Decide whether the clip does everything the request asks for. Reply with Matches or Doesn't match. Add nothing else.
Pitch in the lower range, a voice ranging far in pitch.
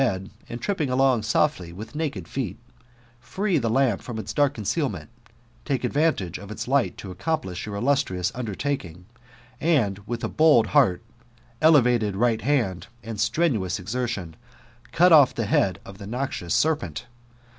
Matches